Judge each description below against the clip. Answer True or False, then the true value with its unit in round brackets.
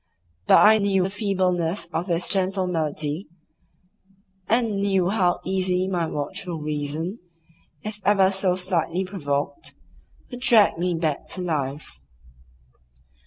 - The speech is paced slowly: True (120 wpm)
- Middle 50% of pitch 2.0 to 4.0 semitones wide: True (3.2 semitones)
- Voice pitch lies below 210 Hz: True (185 Hz)